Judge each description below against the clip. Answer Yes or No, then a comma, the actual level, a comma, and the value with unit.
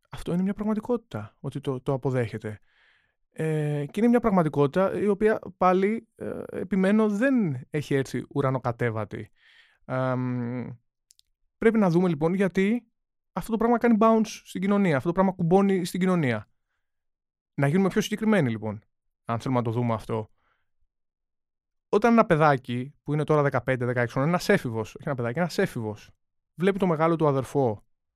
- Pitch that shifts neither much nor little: No, wide, 8.2 semitones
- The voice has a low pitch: No, medium, 145 Hz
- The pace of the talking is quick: No, average, 150 wpm